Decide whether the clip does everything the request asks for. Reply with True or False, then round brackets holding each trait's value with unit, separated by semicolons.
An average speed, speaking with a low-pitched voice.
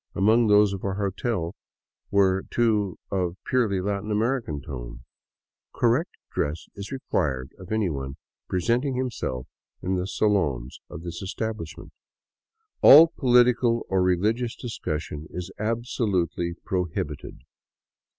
False (120 wpm; 100 Hz)